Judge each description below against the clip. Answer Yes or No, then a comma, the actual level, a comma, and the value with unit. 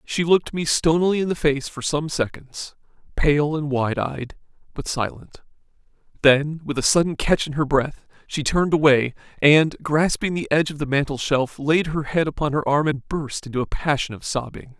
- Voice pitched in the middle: Yes, medium, 150 Hz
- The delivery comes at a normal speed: Yes, average, 195 wpm